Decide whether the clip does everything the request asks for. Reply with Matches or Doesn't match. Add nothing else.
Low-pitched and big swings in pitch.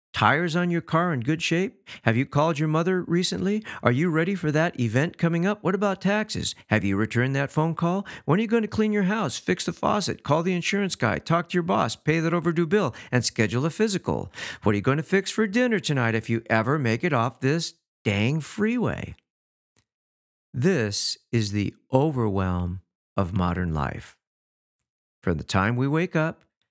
Doesn't match